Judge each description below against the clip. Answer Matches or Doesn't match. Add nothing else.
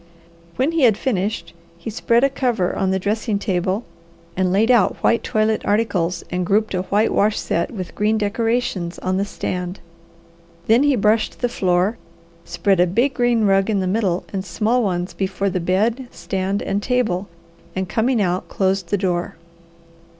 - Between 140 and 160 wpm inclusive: Doesn't match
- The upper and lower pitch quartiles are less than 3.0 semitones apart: Doesn't match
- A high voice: Matches